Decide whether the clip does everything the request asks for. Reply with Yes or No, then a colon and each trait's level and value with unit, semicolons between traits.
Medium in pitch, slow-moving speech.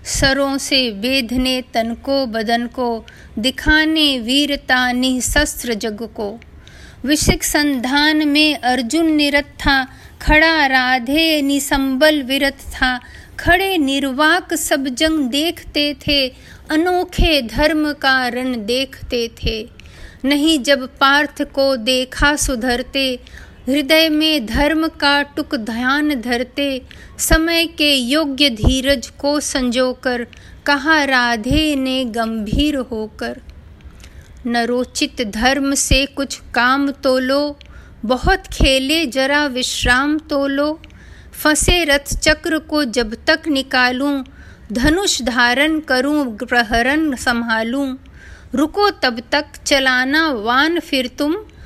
No: very high, 275 Hz; slow, 105 wpm